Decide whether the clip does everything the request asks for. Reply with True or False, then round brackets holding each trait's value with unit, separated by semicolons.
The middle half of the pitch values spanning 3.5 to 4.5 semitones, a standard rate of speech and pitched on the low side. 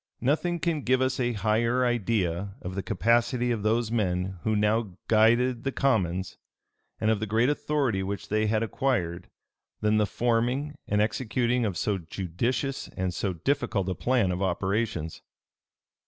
True (4.2 semitones; 155 wpm; 110 Hz)